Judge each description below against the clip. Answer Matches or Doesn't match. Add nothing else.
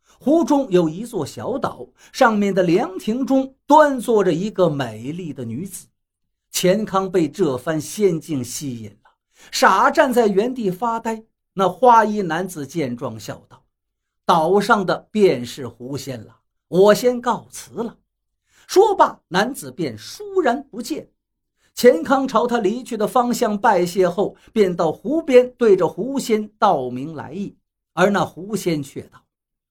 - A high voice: Matches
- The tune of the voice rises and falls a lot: Matches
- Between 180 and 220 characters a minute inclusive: Matches